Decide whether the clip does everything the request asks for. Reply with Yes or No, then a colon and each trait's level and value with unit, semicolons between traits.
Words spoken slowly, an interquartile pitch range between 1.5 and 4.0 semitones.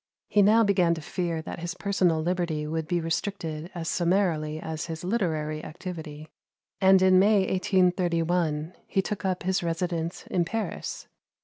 No: average, 150 wpm; average, 2.7 semitones